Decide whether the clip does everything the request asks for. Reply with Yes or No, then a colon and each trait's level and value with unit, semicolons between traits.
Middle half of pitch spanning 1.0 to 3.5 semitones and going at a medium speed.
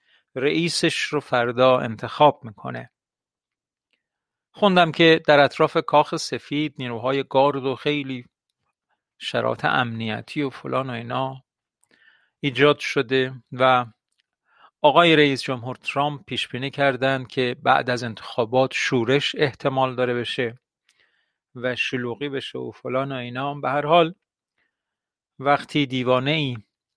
Yes: average, 2.8 semitones; average, 115 wpm